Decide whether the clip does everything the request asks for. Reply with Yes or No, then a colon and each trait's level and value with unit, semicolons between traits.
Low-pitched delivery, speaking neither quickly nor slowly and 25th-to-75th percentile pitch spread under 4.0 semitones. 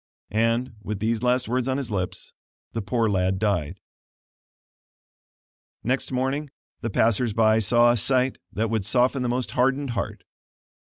Yes: low, 115 Hz; average, 150 wpm; average, 2.9 semitones